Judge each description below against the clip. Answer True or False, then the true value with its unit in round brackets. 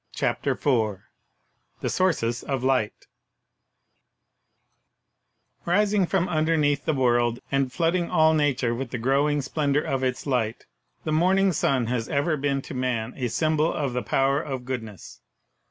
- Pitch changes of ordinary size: True (3.9 semitones)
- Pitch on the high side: False (135 Hz)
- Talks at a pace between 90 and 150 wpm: True (145 wpm)